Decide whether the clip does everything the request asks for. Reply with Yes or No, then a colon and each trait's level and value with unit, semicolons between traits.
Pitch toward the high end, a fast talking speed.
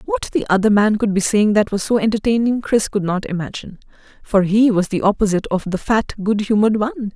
Yes: high, 215 Hz; fast, 220 wpm